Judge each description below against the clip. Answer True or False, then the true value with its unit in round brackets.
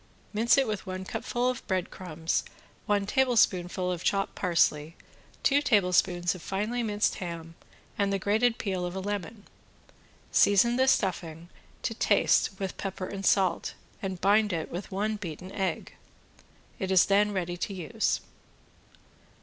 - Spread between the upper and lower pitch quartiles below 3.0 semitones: True (2.6 semitones)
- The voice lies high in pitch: True (195 Hz)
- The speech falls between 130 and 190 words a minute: True (150 wpm)